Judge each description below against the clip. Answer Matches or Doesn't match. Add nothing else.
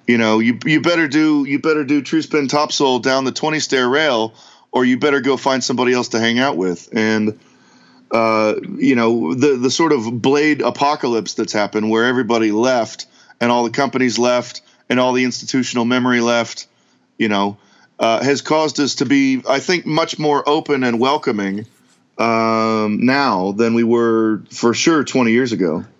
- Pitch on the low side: Matches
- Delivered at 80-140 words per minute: Doesn't match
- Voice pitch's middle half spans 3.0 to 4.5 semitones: Matches